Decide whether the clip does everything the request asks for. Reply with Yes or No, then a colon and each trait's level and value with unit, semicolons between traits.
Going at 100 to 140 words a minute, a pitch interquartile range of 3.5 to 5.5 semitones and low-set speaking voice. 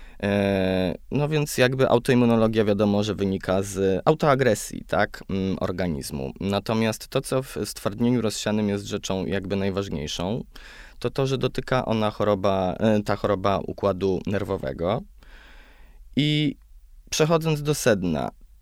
Yes: average, 115 wpm; average, 4.1 semitones; low, 105 Hz